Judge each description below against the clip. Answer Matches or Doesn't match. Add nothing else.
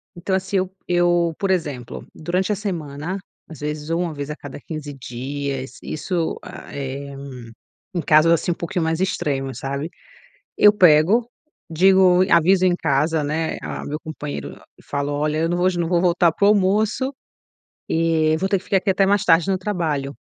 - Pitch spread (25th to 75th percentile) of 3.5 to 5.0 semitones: Matches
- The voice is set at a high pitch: Doesn't match